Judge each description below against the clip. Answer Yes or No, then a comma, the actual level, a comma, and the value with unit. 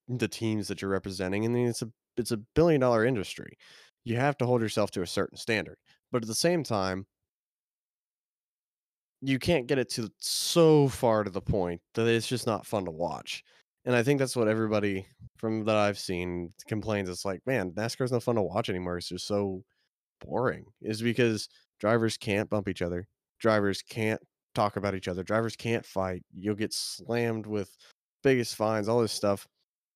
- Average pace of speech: Yes, average, 190 wpm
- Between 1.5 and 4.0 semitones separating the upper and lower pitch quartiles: Yes, average, 3.4 semitones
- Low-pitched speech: Yes, low, 110 Hz